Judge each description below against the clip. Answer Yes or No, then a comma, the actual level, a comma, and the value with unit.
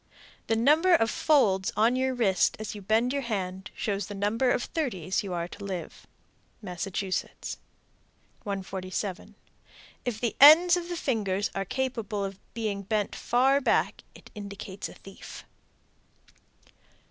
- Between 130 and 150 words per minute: Yes, average, 140 wpm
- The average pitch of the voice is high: Yes, high, 210 Hz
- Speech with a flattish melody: No, average, 4.5 semitones